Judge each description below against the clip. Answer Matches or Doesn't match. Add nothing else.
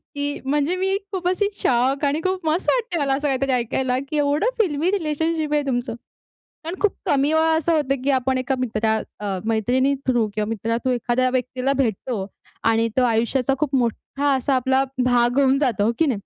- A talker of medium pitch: Doesn't match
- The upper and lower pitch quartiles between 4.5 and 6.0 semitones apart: Doesn't match